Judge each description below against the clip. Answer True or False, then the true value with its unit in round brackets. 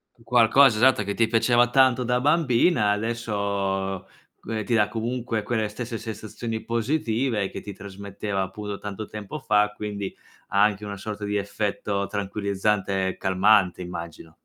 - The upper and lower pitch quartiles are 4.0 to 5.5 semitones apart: False (2.6 semitones)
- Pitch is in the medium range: False (105 Hz)